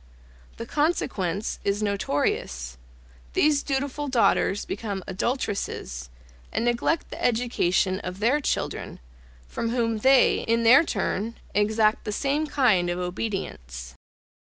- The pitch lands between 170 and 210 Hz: No, high, 220 Hz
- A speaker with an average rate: No, slow, 115 wpm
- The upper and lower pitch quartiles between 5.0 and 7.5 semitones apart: Yes, average, 5.3 semitones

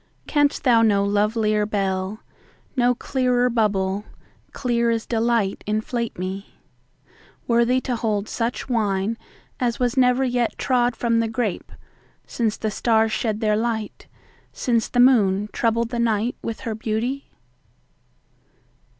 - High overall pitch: Yes, high, 230 Hz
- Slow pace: Yes, slow, 115 wpm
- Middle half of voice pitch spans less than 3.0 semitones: Yes, narrow, 2.4 semitones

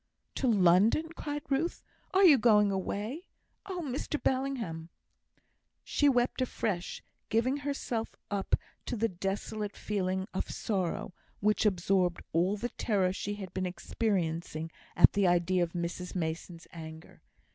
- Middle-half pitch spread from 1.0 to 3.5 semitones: No, wide, 5.4 semitones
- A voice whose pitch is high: Yes, high, 200 Hz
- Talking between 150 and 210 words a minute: No, slow, 135 wpm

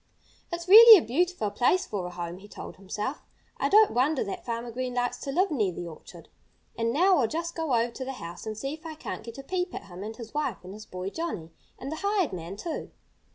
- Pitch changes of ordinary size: No, wide, 8.1 semitones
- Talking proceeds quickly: Yes, fast, 245 wpm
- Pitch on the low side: No, high, 245 Hz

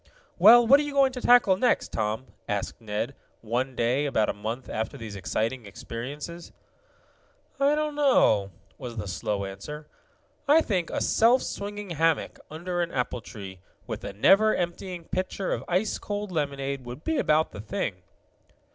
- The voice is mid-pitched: Yes, medium, 150 Hz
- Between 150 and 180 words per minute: Yes, average, 165 wpm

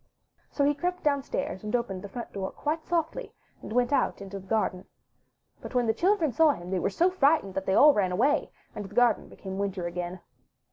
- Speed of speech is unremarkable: No, fast, 215 wpm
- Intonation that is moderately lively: No, wide, 7.5 semitones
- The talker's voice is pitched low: No, high, 230 Hz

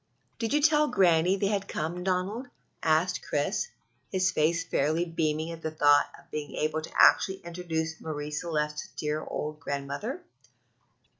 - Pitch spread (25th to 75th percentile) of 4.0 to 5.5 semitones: No, average, 3.5 semitones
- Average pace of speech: Yes, average, 160 wpm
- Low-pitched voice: No, medium, 165 Hz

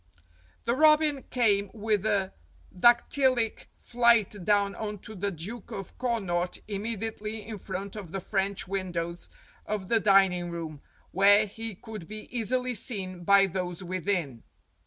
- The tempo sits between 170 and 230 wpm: No, slow, 135 wpm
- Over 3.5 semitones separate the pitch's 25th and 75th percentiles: No, average, 3.2 semitones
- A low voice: No, high, 200 Hz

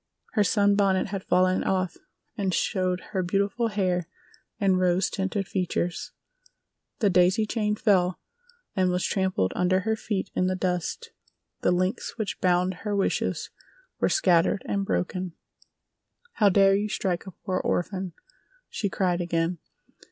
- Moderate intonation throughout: No, narrow, 2.0 semitones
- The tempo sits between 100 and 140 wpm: Yes, slow, 135 wpm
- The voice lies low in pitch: No, medium, 185 Hz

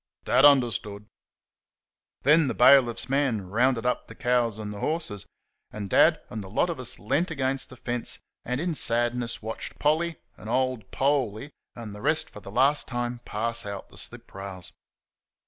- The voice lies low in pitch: Yes, low, 120 Hz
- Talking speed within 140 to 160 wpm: No, average, 170 wpm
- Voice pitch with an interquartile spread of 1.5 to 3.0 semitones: No, average, 4.3 semitones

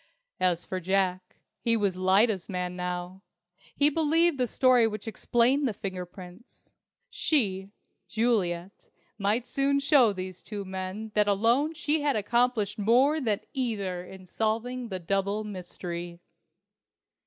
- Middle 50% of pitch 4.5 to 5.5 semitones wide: Yes, average, 4.9 semitones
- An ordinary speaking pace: No, slow, 130 wpm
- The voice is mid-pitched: No, high, 210 Hz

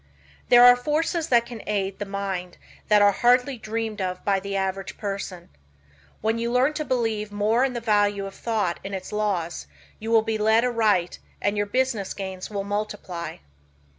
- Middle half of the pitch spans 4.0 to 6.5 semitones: No, average, 3.1 semitones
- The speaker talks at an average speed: Yes, average, 180 wpm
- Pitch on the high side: Yes, high, 210 Hz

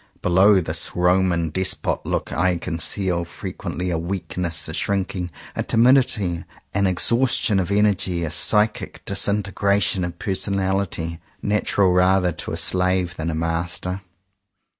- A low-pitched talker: Yes, very low, 90 Hz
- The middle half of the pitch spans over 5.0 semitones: No, narrow, 2.5 semitones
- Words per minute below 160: Yes, average, 140 wpm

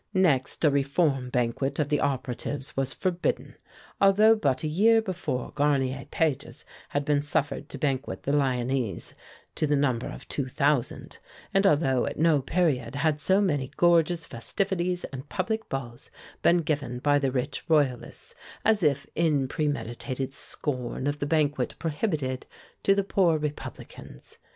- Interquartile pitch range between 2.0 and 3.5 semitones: No, average, 4.0 semitones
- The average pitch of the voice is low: No, medium, 145 Hz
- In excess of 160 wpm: No, average, 150 wpm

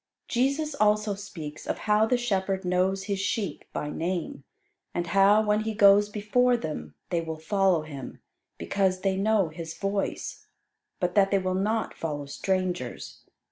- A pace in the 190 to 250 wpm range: No, average, 155 wpm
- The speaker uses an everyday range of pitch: Yes, average, 3.3 semitones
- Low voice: No, high, 195 Hz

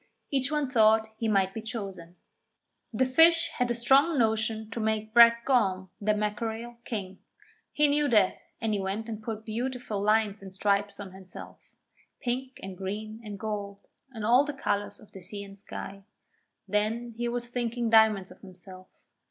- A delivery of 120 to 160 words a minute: No, average, 170 wpm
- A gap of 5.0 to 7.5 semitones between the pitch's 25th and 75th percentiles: No, average, 3.0 semitones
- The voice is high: Yes, high, 220 Hz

